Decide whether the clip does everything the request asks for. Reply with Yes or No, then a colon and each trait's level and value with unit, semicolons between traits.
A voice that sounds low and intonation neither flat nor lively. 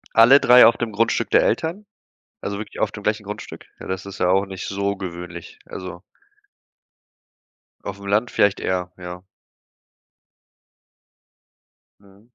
Yes: low, 100 Hz; average, 3.4 semitones